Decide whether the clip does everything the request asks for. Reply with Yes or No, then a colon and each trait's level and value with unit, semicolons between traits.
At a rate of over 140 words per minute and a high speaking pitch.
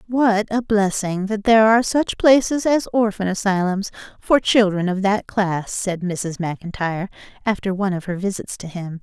Yes: average, 175 wpm; high, 200 Hz